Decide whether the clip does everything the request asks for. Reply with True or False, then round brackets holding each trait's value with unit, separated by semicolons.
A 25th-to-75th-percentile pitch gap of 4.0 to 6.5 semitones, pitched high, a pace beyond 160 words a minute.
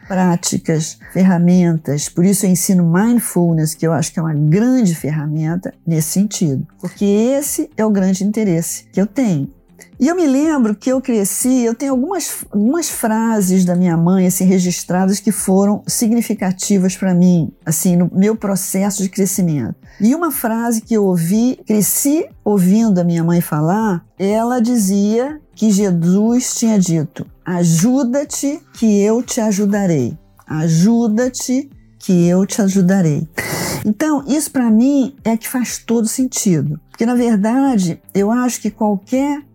False (5.0 semitones; 200 Hz; 150 wpm)